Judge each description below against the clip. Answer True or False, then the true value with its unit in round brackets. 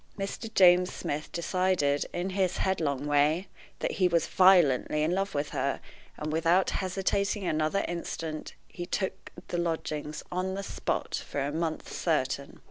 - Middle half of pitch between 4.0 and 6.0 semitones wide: False (3.5 semitones)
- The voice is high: False (170 Hz)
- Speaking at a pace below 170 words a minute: True (150 wpm)